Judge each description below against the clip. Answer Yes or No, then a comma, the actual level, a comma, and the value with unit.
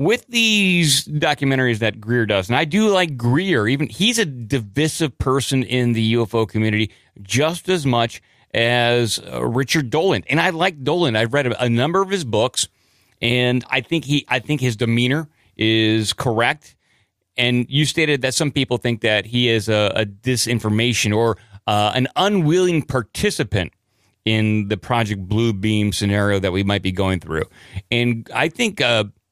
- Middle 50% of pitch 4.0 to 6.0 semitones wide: Yes, average, 5.2 semitones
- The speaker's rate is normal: Yes, average, 170 wpm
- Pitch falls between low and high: No, low, 120 Hz